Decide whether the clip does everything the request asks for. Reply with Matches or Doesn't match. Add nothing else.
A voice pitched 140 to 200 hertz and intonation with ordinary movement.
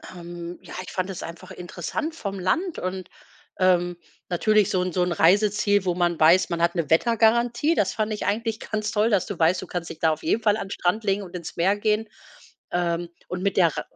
Matches